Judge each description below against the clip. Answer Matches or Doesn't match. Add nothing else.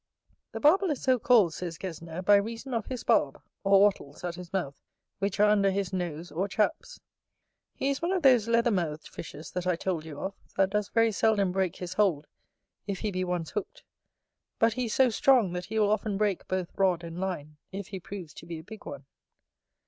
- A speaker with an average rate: Doesn't match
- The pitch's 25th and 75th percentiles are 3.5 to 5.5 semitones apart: Matches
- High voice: Matches